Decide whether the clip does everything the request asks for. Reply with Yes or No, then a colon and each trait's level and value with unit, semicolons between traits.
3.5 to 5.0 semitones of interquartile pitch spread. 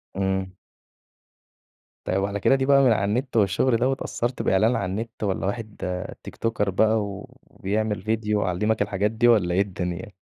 No: average, 2.8 semitones